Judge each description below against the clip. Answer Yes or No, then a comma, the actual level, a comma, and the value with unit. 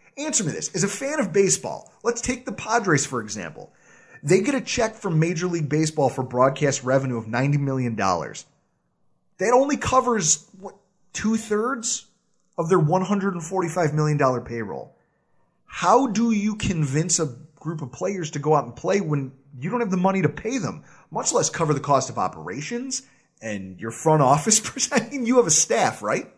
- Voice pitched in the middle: Yes, medium, 180 Hz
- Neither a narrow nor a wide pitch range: No, wide, 7.2 semitones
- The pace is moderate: Yes, average, 175 wpm